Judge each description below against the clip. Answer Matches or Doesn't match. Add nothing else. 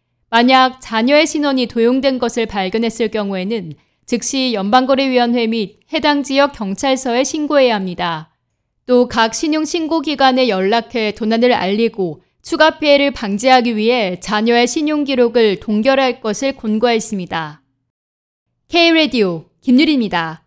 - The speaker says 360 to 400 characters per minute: Doesn't match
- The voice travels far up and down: Doesn't match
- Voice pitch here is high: Matches